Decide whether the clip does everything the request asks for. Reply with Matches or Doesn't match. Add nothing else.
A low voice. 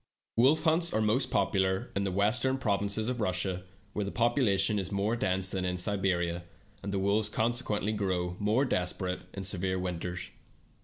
Matches